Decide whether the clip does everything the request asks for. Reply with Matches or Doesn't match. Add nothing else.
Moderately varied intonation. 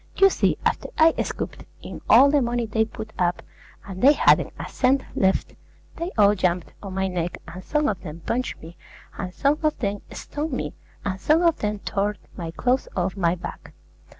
Doesn't match